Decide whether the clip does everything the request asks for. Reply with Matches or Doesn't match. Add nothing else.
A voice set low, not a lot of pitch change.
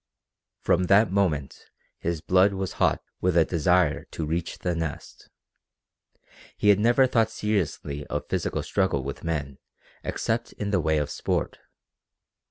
Doesn't match